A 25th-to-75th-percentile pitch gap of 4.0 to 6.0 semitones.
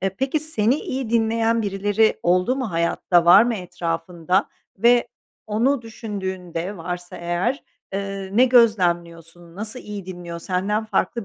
Yes: average, 4.5 semitones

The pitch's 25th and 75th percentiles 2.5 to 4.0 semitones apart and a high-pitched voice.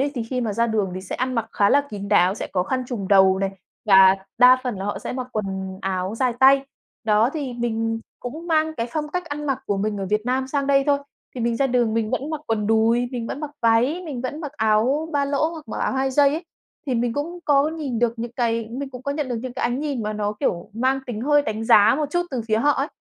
No: average, 4.5 semitones; high, 245 Hz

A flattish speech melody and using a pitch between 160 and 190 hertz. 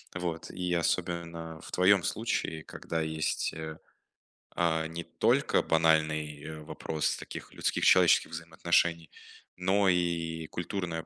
No: narrow, 1.5 semitones; very low, 80 Hz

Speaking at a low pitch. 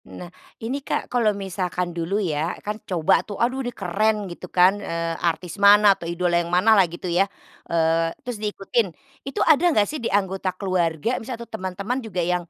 No: high, 190 Hz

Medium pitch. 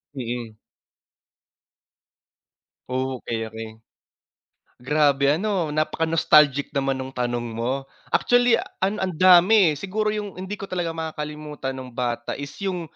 Yes: medium, 150 Hz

